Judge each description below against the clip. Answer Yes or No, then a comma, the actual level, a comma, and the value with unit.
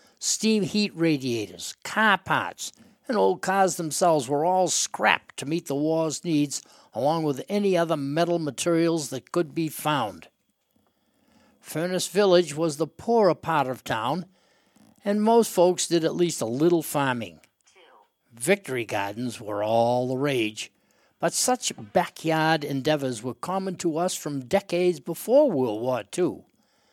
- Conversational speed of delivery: Yes, average, 145 wpm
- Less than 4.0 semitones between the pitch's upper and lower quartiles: No, average, 4.6 semitones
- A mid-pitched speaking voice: Yes, medium, 165 Hz